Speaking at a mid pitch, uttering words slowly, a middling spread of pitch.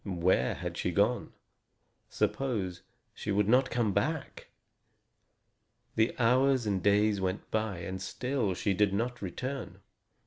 No: low, 105 Hz; slow, 130 wpm; average, 4.5 semitones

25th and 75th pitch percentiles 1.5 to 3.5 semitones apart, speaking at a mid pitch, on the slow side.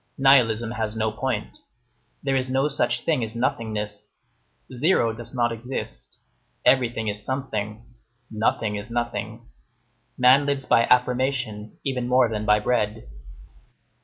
No: average, 3.1 semitones; low, 120 Hz; slow, 130 wpm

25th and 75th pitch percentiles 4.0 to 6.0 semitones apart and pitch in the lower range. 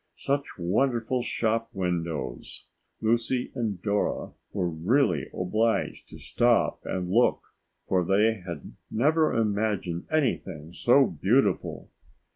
Yes: average, 5.0 semitones; low, 110 Hz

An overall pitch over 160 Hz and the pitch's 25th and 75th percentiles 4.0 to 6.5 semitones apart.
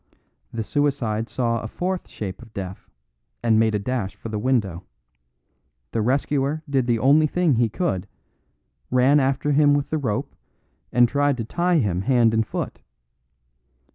No: low, 125 Hz; average, 4.6 semitones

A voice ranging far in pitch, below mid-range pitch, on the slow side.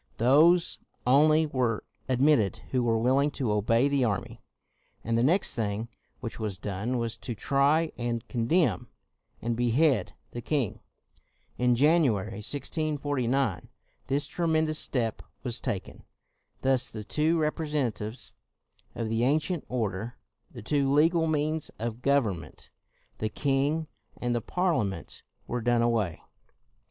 No: average, 4.6 semitones; low, 125 Hz; slow, 130 wpm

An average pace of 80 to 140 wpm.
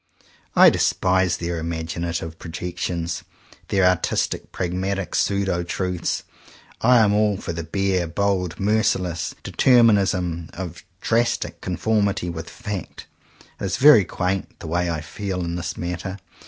Yes: slow, 135 wpm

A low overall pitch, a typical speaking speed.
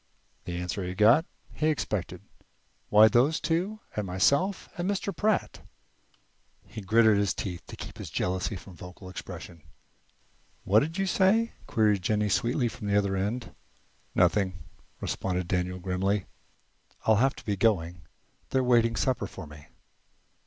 Yes: low, 105 Hz; average, 145 wpm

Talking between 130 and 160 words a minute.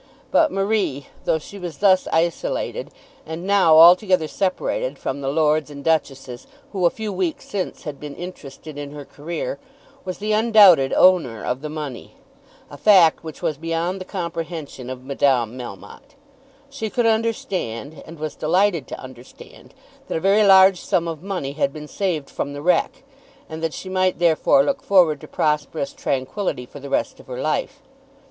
No: average, 170 wpm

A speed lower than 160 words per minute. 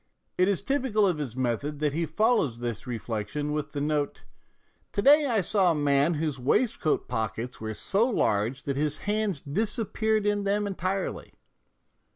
No: average, 165 wpm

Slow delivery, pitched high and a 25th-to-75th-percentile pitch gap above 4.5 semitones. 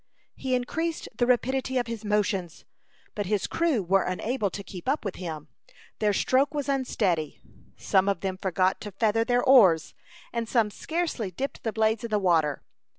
No: average, 175 wpm; high, 215 Hz; average, 5.1 semitones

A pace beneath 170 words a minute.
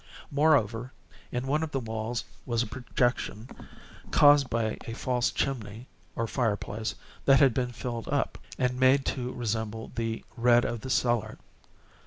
Yes: average, 150 wpm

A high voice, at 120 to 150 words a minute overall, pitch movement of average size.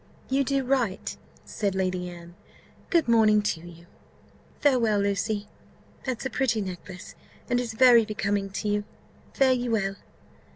Yes: high, 215 Hz; average, 140 wpm; average, 4.1 semitones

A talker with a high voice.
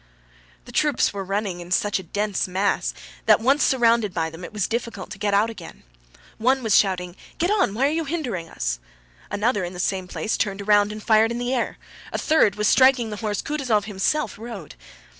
Yes: high, 210 Hz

